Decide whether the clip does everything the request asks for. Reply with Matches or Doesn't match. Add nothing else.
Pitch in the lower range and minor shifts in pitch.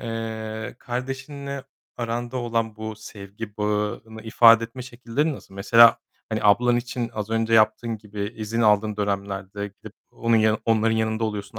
Matches